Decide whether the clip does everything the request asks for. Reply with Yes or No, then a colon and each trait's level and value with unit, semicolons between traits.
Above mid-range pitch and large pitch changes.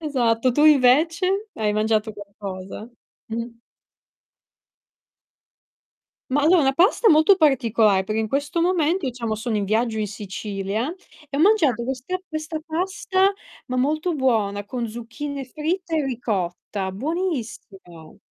Yes: very high, 255 Hz; wide, 6.5 semitones